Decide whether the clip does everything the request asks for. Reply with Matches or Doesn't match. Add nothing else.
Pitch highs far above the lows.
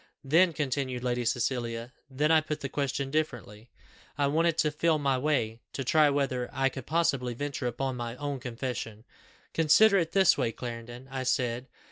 Doesn't match